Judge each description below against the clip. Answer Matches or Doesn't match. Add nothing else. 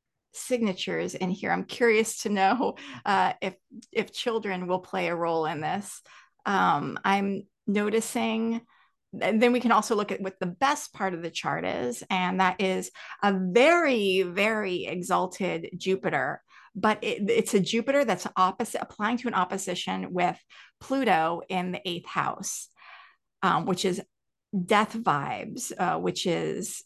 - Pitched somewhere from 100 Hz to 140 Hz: Doesn't match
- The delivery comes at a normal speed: Matches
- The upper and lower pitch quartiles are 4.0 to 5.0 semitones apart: Doesn't match